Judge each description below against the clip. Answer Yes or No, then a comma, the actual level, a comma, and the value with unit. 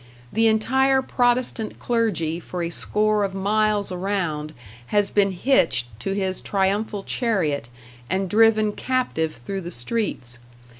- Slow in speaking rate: Yes, slow, 130 wpm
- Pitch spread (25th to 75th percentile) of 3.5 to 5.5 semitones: Yes, average, 3.9 semitones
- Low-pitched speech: No, high, 200 Hz